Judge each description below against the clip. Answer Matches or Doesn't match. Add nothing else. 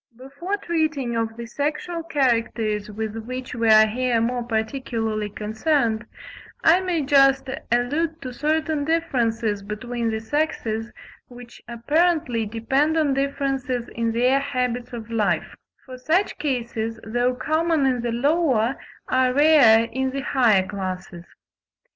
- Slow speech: Matches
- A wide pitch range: Doesn't match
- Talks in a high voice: Matches